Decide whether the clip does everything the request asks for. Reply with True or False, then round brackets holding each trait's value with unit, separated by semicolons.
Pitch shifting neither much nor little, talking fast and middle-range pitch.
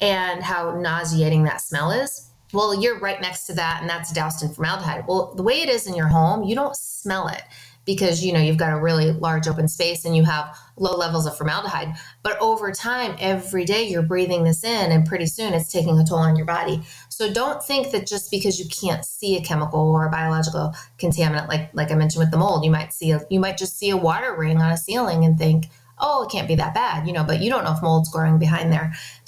True (3.2 semitones; 245 wpm; 165 Hz)